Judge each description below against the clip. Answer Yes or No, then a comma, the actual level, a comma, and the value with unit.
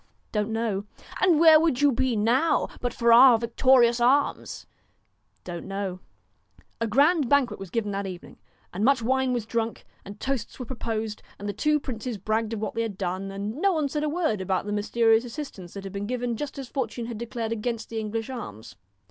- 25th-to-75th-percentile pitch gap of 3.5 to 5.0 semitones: Yes, average, 4.0 semitones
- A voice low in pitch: No, high, 230 Hz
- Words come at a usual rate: No, fast, 210 wpm